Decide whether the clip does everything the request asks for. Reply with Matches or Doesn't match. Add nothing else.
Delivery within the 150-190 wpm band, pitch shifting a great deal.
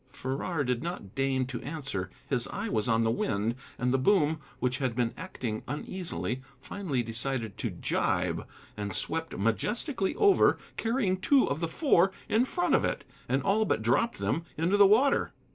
Matches